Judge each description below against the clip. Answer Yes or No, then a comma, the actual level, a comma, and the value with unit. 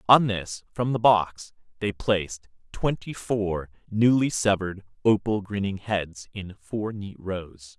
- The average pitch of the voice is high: No, low, 100 Hz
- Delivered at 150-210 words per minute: No, average, 140 wpm